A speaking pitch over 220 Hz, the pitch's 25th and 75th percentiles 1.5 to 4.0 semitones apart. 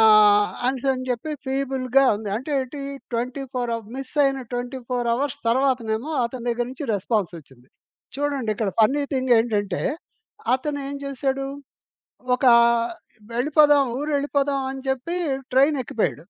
Yes: very high, 255 Hz; average, 3.0 semitones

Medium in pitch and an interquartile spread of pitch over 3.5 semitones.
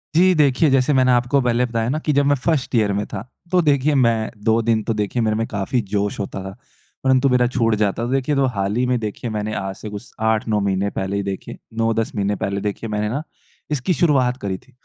No: low, 115 Hz; average, 4.2 semitones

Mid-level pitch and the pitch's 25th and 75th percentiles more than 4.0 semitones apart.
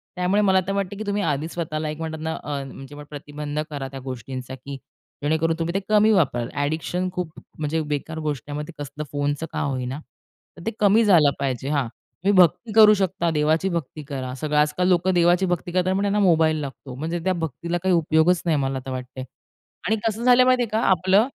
Yes: medium, 160 Hz; average, 4.4 semitones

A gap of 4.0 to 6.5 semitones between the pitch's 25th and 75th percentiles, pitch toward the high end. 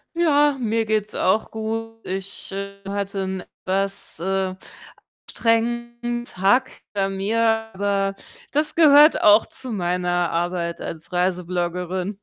No: average, 3.6 semitones; high, 200 Hz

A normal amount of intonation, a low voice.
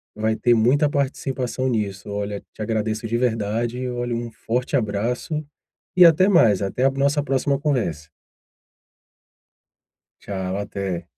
Yes: average, 4.6 semitones; low, 120 Hz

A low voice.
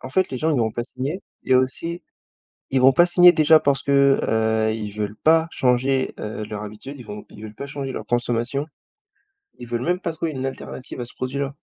Yes: low, 130 Hz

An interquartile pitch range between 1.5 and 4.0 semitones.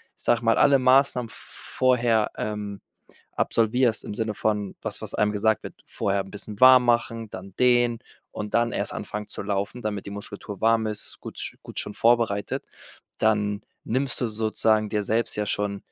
Yes: narrow, 2.4 semitones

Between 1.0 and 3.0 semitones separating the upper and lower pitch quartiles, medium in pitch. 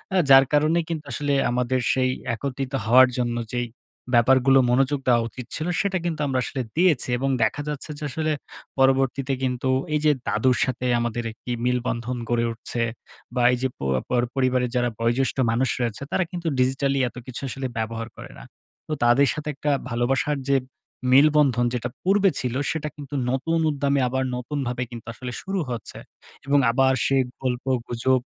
No: narrow, 2.6 semitones; low, 130 Hz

